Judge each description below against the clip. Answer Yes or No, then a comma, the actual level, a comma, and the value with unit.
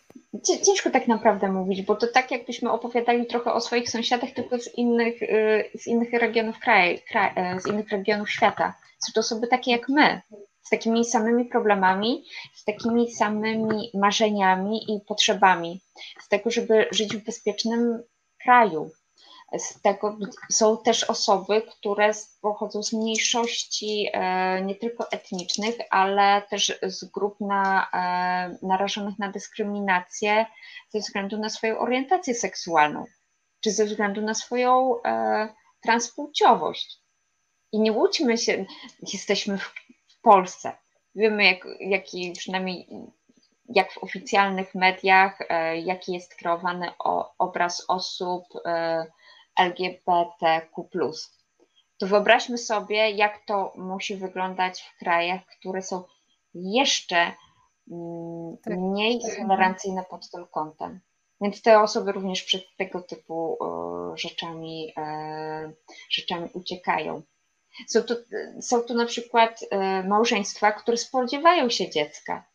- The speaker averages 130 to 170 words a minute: No, average, 120 wpm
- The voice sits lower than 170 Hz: No, high, 210 Hz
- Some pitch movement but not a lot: Yes, average, 3.7 semitones